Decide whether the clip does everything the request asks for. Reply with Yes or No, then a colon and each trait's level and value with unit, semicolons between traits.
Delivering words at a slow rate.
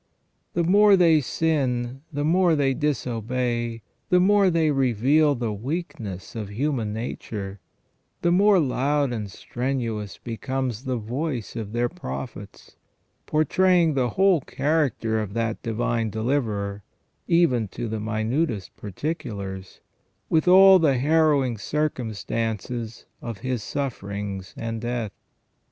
Yes: slow, 120 wpm